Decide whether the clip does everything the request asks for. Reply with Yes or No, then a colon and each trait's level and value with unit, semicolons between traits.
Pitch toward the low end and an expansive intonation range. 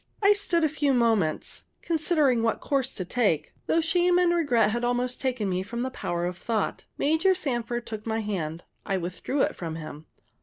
No: high, 240 Hz; wide, 7.6 semitones